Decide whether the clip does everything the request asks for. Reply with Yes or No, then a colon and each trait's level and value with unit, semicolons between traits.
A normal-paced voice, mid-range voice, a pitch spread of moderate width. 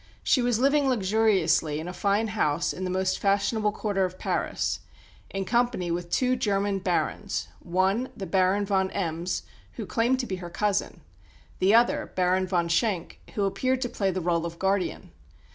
No: average, 175 wpm; high, 195 Hz; average, 3.4 semitones